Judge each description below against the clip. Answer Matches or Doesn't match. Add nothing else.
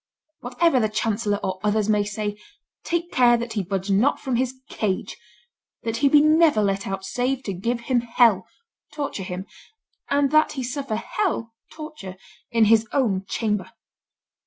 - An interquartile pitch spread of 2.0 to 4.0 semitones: Doesn't match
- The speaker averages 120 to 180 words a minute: Matches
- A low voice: Doesn't match